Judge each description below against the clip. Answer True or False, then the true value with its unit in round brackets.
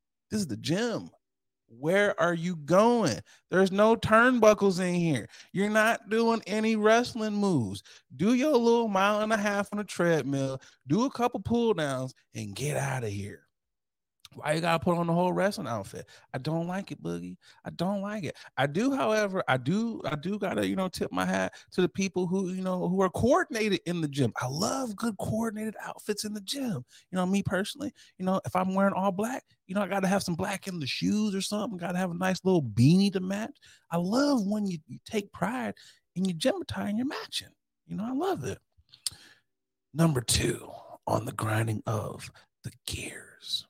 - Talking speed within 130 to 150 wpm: False (200 wpm)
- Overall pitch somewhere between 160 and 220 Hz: True (190 Hz)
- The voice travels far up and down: True (5.7 semitones)